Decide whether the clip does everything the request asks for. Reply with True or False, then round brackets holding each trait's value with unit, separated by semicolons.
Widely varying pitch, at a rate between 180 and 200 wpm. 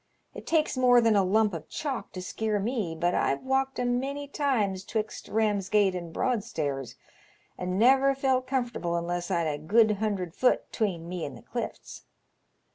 False (6.1 semitones; 170 wpm)